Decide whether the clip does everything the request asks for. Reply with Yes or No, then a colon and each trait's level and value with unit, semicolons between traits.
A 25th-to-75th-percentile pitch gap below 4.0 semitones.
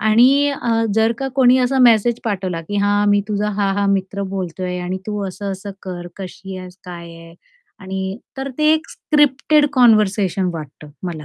No: average, 4.6 semitones